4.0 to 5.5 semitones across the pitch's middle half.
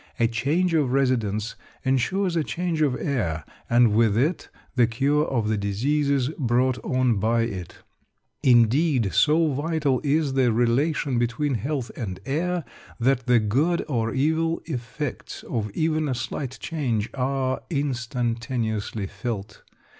Yes: average, 4.4 semitones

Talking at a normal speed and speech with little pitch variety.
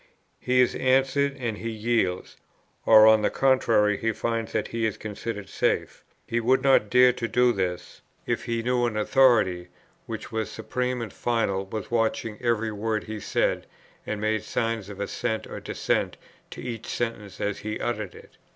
Yes: average, 175 wpm; narrow, 2.3 semitones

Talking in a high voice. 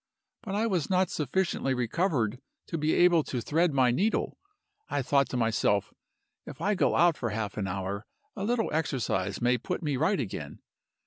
No: medium, 140 Hz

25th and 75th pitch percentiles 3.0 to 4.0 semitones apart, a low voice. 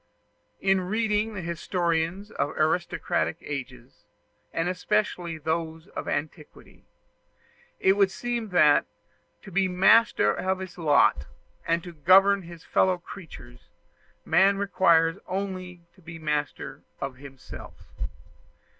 No: average, 3.3 semitones; medium, 175 Hz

